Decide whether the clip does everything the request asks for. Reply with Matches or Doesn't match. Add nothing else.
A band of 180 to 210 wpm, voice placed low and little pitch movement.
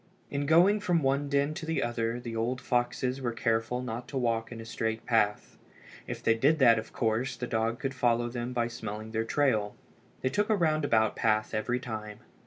Doesn't match